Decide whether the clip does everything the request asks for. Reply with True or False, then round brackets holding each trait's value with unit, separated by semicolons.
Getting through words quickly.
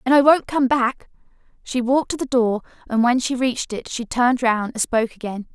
True (225 wpm)